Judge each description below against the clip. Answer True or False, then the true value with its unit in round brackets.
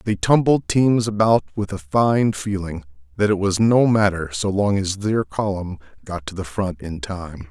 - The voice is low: True (100 Hz)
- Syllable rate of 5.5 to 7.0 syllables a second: False (4.4 syllables/s)